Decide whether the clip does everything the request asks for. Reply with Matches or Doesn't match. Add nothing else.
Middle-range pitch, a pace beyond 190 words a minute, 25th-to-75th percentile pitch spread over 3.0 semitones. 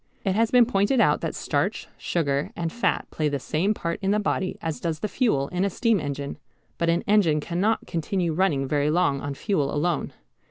Matches